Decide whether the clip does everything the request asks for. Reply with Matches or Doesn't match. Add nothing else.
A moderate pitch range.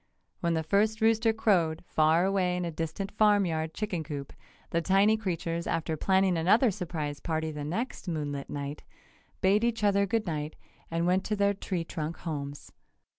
Matches